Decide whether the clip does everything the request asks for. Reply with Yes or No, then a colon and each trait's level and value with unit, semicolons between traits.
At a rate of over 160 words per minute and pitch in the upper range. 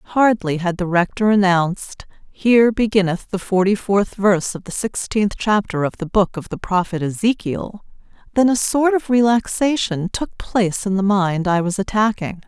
Yes: average, 170 wpm; high, 200 Hz